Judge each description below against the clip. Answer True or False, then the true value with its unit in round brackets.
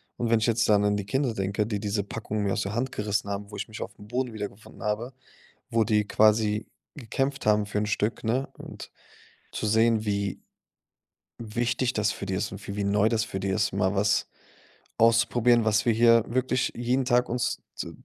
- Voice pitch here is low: True (110 Hz)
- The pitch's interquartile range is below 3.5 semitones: True (2.4 semitones)